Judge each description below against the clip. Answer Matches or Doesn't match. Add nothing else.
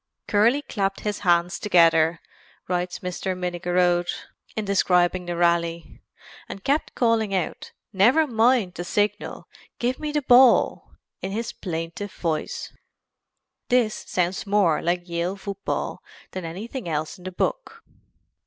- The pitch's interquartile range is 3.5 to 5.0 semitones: Matches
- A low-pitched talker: Doesn't match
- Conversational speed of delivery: Doesn't match